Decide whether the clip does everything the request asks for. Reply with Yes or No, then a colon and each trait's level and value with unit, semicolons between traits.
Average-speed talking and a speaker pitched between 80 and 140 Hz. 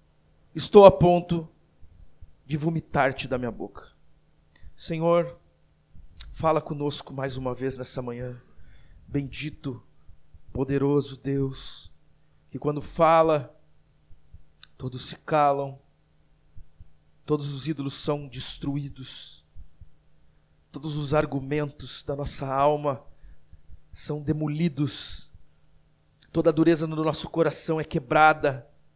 No: slow, 95 wpm; low, 135 Hz